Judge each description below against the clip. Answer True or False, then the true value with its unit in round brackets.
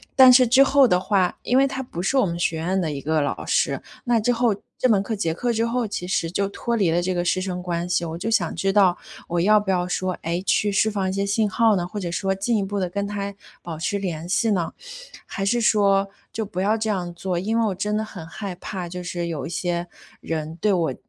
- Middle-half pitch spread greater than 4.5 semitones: False (3.6 semitones)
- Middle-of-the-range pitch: False (195 Hz)